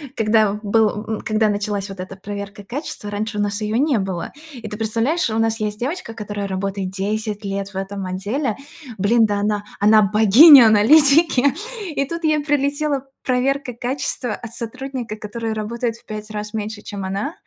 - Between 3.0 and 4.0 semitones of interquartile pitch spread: Yes, average, 3.4 semitones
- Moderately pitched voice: No, high, 215 Hz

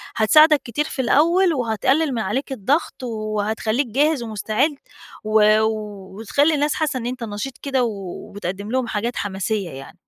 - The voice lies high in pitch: Yes, high, 230 Hz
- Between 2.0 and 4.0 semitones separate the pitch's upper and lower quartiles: No, average, 4.8 semitones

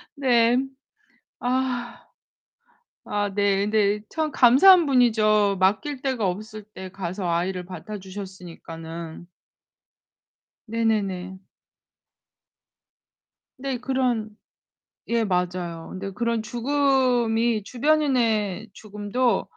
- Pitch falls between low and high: No, high, 215 Hz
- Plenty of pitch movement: No, average, 4.5 semitones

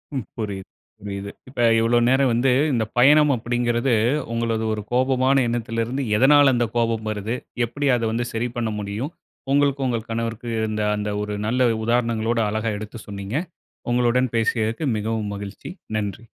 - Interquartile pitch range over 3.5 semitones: No, narrow, 2.4 semitones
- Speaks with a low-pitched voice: Yes, low, 115 Hz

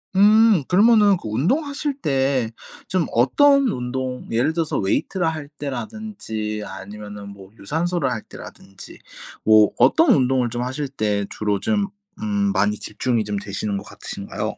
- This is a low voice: Yes, low, 130 Hz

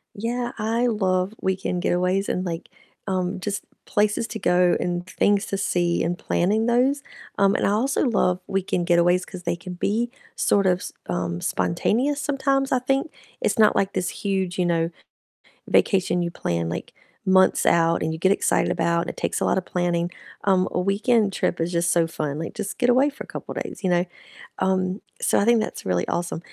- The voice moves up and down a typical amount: Yes, average, 3.5 semitones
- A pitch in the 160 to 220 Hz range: Yes, medium, 185 Hz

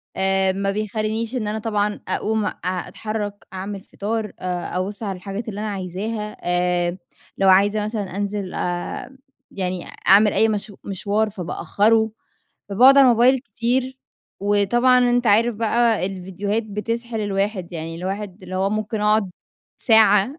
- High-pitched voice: Yes, high, 205 Hz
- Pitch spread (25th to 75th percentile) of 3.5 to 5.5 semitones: No, narrow, 2.4 semitones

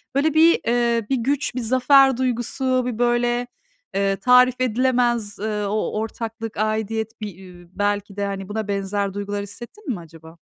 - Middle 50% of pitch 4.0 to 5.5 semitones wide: No, average, 3.6 semitones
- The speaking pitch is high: Yes, high, 225 Hz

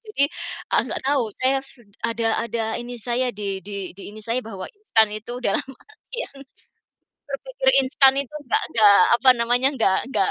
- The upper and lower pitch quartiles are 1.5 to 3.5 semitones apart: No, average, 4.1 semitones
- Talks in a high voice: Yes, high, 240 Hz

